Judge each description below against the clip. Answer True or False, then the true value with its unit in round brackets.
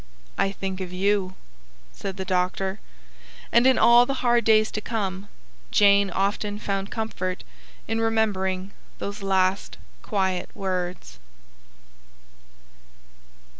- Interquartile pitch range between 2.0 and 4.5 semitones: True (2.5 semitones)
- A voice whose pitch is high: True (195 Hz)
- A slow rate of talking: True (110 wpm)